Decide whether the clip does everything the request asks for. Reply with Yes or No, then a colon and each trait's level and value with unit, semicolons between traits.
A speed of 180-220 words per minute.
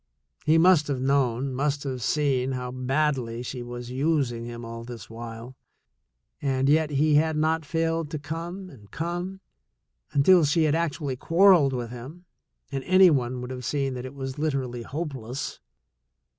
No: average, 160 wpm